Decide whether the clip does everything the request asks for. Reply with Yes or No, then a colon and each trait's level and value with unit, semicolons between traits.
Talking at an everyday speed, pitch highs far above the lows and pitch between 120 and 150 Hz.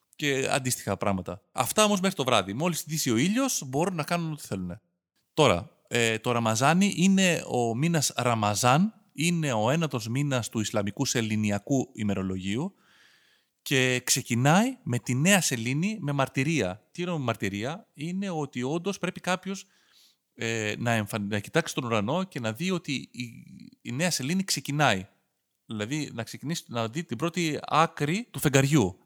Yes: average, 155 wpm; wide, 7.0 semitones; medium, 140 Hz